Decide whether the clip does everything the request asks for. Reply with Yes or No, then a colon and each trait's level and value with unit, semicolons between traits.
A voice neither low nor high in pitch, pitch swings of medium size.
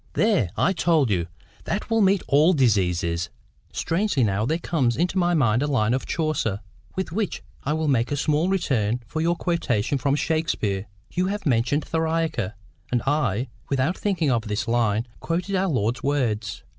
No: medium, 145 Hz; wide, 6.8 semitones